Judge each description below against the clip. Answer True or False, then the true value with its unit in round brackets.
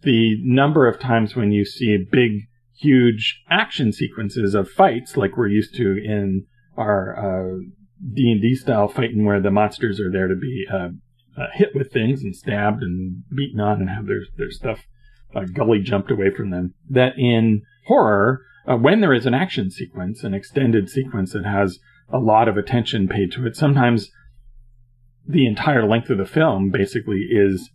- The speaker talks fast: False (175 wpm)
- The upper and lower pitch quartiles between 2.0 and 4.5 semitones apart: True (4.2 semitones)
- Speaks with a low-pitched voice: True (115 Hz)